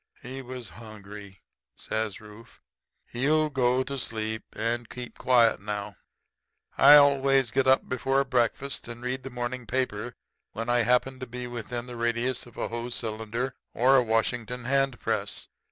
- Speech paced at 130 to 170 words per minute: Yes, average, 155 wpm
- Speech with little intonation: Yes, narrow, 2.3 semitones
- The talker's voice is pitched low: Yes, low, 120 Hz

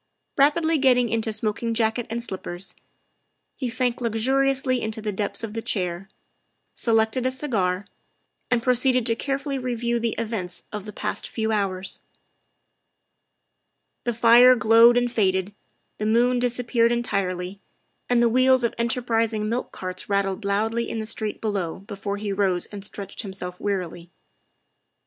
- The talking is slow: No, average, 150 wpm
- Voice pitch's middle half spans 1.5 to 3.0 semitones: No, average, 3.4 semitones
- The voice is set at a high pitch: Yes, high, 225 Hz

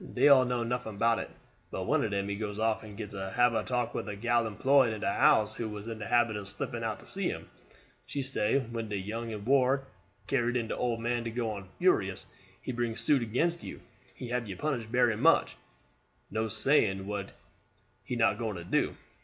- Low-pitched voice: Yes, low, 115 Hz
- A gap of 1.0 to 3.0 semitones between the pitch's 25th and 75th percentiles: Yes, average, 2.7 semitones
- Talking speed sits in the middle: No, fast, 220 wpm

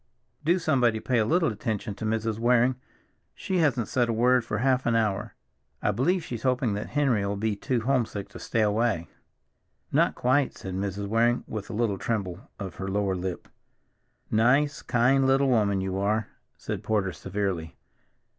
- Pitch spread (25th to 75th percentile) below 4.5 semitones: Yes, average, 4.0 semitones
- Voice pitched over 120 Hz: No, low, 110 Hz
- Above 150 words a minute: Yes, average, 170 wpm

